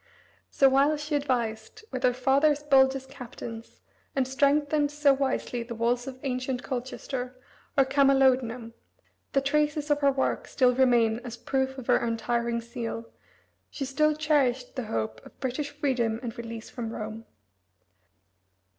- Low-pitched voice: No, very high, 260 Hz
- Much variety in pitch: No, average, 2.9 semitones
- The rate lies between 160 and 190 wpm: No, average, 145 wpm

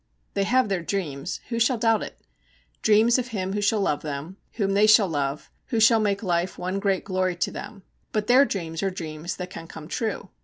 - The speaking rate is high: Yes, fast, 215 wpm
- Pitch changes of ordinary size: Yes, average, 3.9 semitones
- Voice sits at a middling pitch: No, high, 195 Hz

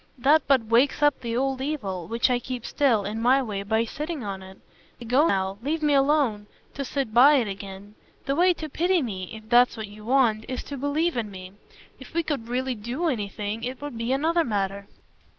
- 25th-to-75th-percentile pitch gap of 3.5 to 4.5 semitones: No, average, 5.0 semitones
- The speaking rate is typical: No, fast, 215 wpm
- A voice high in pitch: Yes, high, 245 Hz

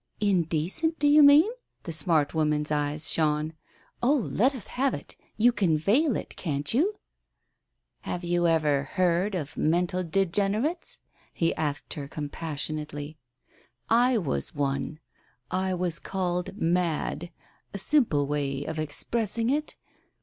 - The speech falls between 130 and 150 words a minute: Yes, average, 145 wpm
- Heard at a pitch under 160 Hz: No, medium, 175 Hz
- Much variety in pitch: Yes, wide, 6.1 semitones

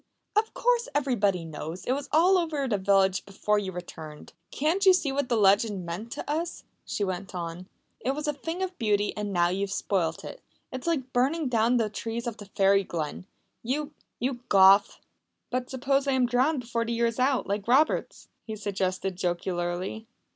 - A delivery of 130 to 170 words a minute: No, average, 190 wpm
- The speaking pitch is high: Yes, high, 225 Hz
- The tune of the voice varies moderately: No, wide, 6.1 semitones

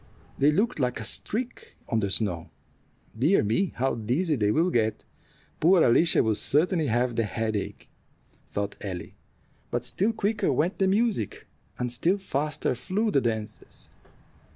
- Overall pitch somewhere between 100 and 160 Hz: Yes, low, 135 Hz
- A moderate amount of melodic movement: No, wide, 9.0 semitones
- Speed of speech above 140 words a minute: Yes, average, 150 wpm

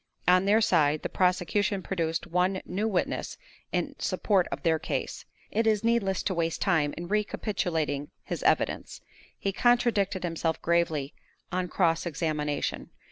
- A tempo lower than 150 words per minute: Yes, average, 140 wpm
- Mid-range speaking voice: Yes, medium, 180 Hz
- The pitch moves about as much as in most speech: Yes, average, 3.5 semitones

